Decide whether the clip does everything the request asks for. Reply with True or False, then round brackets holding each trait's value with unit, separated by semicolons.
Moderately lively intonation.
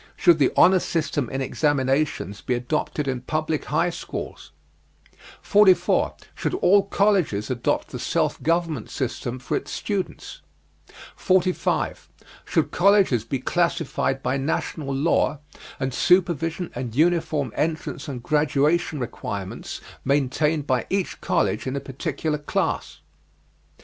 True (4.6 semitones)